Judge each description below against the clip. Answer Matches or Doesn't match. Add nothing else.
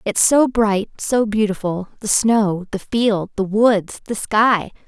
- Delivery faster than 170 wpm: Doesn't match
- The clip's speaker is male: Doesn't match